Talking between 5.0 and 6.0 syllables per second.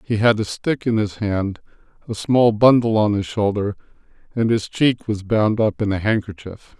No: 4.6 syllables/s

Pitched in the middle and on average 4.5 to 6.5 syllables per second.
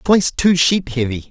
Yes: medium, 155 Hz; 5.0 syllables/s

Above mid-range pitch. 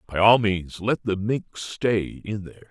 No: low, 105 Hz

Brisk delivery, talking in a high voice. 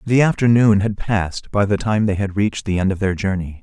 No: fast, 250 wpm; low, 100 Hz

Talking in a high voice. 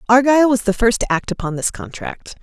Yes: high, 230 Hz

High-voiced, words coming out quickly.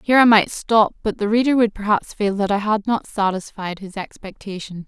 Yes: high, 205 Hz; fast, 210 wpm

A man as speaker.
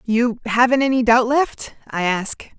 No: female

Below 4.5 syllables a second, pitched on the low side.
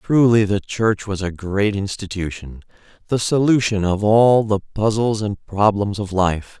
Yes: 4.2 syllables/s; low, 105 Hz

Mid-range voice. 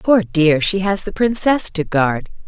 Yes: medium, 180 Hz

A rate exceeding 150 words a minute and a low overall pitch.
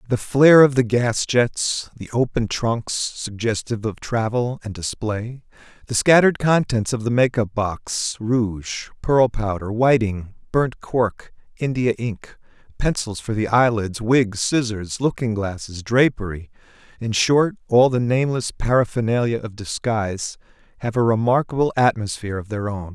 No: slow, 135 wpm; low, 115 Hz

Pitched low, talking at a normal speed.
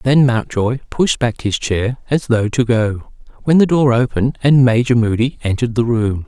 Yes: low, 120 Hz; average, 190 wpm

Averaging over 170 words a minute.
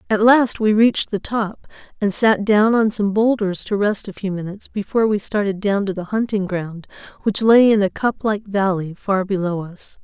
Yes: fast, 205 wpm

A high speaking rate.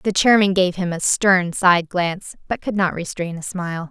Yes: fast, 215 wpm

